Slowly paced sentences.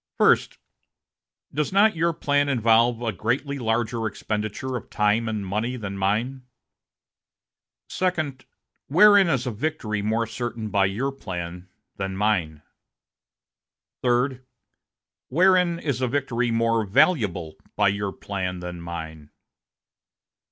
Yes: slow, 115 wpm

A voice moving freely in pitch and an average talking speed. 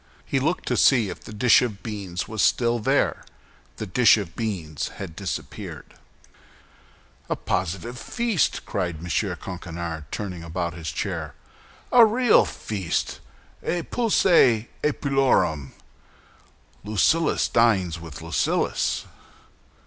No: wide, 6.7 semitones; slow, 115 wpm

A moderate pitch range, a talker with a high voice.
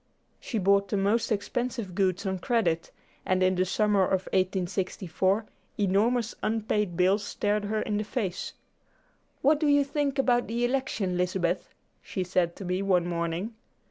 Yes: average, 3.4 semitones; high, 200 Hz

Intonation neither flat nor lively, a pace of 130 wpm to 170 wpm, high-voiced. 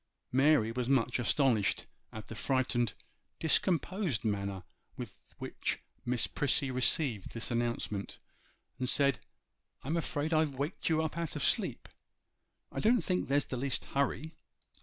No: average, 4.7 semitones; average, 140 wpm; low, 135 Hz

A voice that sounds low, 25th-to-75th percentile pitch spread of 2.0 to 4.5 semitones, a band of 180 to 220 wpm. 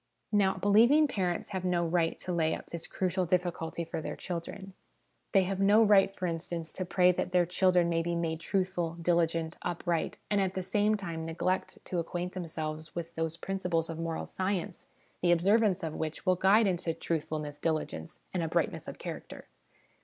No: medium, 175 Hz; narrow, 2.4 semitones; average, 185 wpm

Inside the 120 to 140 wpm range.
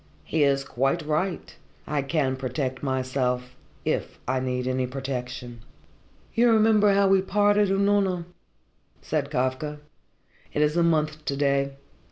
Yes: slow, 135 wpm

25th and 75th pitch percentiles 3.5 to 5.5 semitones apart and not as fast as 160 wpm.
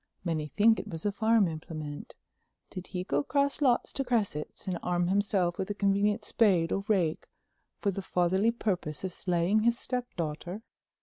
No: average, 4.0 semitones; average, 170 wpm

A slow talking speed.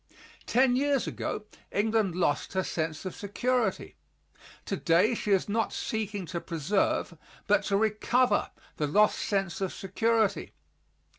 Yes: slow, 130 wpm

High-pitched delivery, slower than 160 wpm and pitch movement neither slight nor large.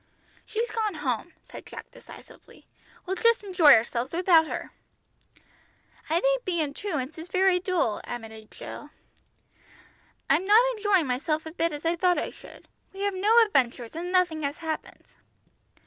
Yes: very high, 340 Hz; average, 150 wpm; average, 4.7 semitones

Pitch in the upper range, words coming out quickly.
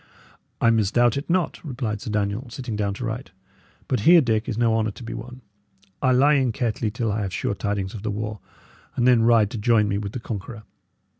No: low, 115 Hz; fast, 220 wpm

